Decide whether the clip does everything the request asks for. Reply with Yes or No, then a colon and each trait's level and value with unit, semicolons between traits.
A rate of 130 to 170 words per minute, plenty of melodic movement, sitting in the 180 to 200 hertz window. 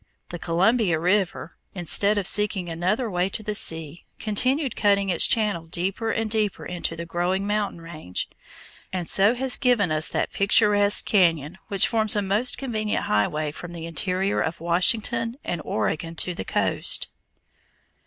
No: average, 155 wpm; average, 4.0 semitones; high, 190 Hz